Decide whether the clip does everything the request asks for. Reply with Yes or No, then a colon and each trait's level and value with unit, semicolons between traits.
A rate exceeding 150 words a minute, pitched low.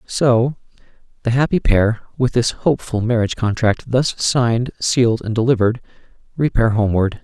No: slow, 135 wpm; low, 120 Hz